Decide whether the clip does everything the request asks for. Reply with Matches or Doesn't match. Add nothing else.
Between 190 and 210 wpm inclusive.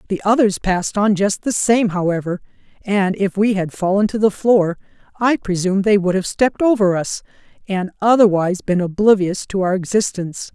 Doesn't match